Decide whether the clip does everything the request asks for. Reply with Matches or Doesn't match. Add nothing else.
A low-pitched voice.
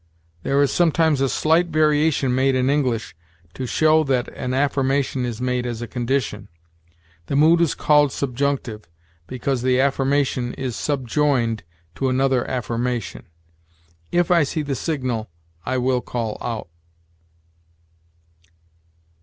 Matches